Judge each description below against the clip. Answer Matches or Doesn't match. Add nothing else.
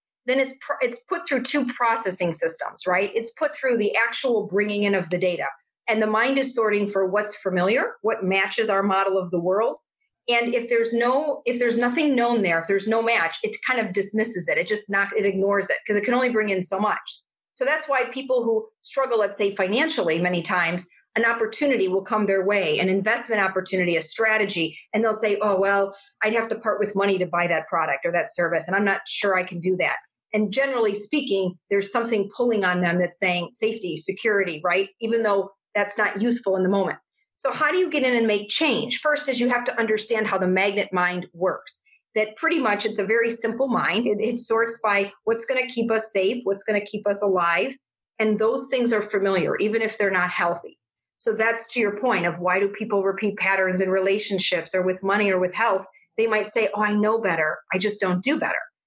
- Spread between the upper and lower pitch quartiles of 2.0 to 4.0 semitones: Matches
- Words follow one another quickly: Matches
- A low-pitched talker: Doesn't match